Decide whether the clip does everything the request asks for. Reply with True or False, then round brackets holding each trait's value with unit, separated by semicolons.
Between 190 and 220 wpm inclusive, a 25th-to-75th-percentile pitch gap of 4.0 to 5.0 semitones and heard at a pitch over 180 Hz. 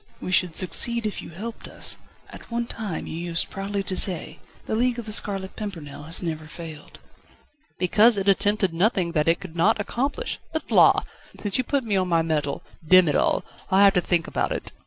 True (205 wpm; 4.3 semitones; 190 Hz)